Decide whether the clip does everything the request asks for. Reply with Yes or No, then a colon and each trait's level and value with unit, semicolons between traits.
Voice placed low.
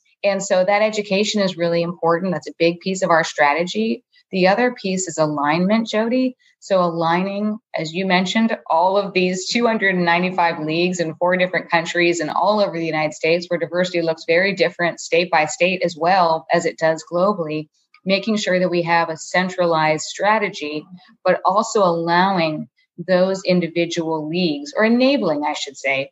No: medium, 175 Hz